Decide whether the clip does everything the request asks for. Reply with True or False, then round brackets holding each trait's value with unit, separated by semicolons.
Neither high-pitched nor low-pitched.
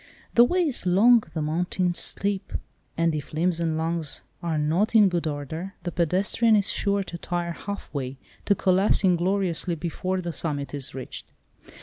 True (175 Hz)